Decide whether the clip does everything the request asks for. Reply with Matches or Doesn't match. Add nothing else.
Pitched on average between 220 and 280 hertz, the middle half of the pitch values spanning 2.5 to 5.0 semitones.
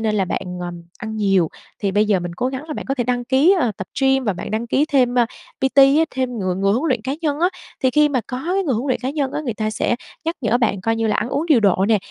Matches